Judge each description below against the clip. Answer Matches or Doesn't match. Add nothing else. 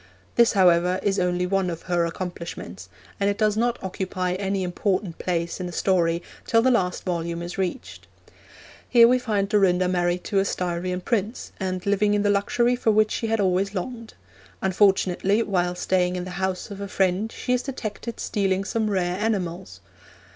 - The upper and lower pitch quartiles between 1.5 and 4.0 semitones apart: Matches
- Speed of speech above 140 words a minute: Matches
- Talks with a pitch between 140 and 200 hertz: Matches